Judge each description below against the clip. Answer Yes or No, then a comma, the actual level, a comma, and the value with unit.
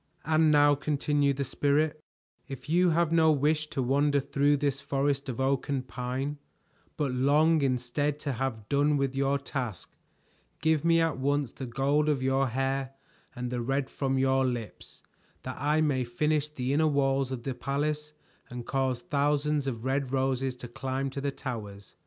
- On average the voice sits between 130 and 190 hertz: Yes, medium, 140 Hz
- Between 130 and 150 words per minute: No, average, 175 wpm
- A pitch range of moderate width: No, narrow, 2.0 semitones